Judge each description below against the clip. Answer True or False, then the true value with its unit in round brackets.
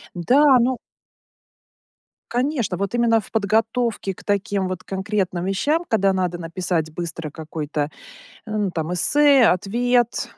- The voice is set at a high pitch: True (195 Hz)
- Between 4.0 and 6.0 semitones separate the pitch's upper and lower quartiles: True (5.0 semitones)